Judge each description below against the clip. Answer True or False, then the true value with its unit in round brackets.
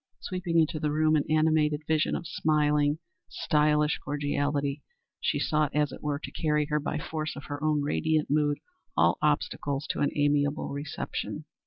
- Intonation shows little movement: True (1.1 semitones)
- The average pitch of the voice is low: False (150 Hz)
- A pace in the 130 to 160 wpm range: False (170 wpm)